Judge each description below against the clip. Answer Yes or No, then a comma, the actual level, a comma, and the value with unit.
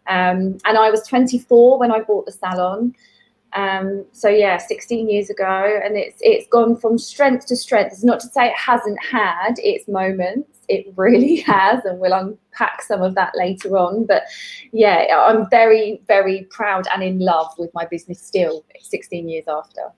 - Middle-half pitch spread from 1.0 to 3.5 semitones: No, average, 4.3 semitones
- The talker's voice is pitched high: Yes, high, 210 Hz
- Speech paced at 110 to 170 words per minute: No, average, 180 wpm